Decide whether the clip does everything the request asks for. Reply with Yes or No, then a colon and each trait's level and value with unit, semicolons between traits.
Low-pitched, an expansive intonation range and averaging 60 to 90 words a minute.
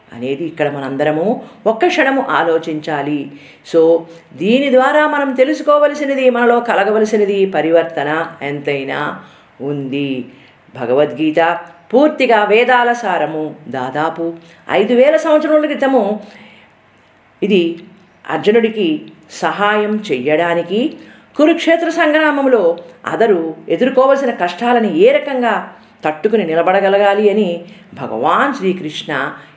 No: high, 200 Hz; wide, 7.9 semitones; average, 85 wpm